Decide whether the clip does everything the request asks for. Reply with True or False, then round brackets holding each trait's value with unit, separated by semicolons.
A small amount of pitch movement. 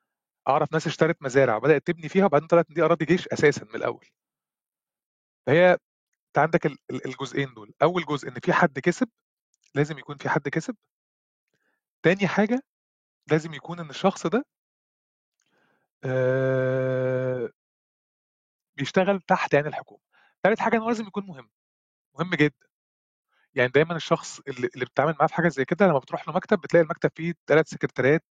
False (4.4 semitones)